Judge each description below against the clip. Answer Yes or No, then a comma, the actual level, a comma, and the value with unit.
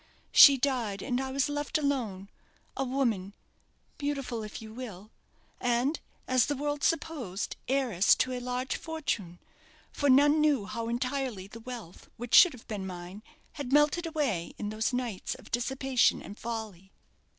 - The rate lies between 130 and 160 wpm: Yes, average, 155 wpm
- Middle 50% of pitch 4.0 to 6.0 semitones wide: Yes, average, 4.7 semitones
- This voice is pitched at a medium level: No, very high, 250 Hz